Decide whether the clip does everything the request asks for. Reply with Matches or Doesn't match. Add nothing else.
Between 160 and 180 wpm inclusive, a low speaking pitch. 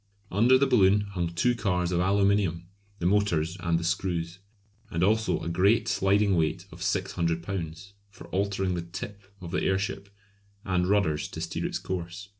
Matches